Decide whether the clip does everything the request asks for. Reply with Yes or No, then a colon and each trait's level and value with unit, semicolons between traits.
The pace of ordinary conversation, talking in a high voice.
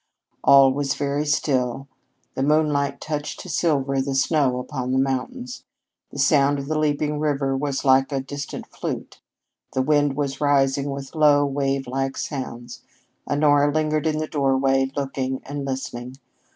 No: average, 150 wpm; medium, 140 Hz